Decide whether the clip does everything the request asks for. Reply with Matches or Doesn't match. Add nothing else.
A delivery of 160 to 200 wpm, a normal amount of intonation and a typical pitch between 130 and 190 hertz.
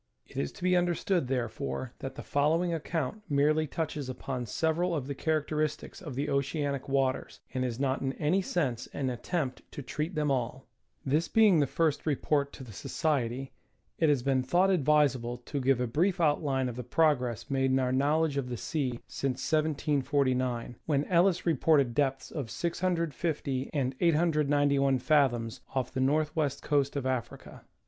Matches